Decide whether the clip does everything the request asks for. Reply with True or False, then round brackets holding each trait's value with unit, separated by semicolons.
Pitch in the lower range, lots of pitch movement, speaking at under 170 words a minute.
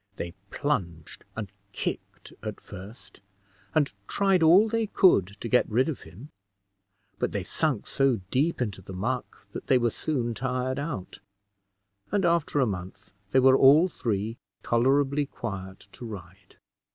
True (125 Hz; 6.3 semitones; 150 wpm)